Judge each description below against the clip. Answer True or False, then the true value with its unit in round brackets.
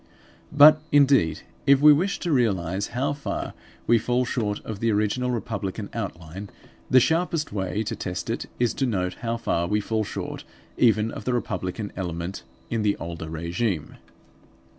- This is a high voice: False (110 Hz)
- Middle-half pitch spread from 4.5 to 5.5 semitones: True (5.2 semitones)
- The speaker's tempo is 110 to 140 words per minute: False (160 wpm)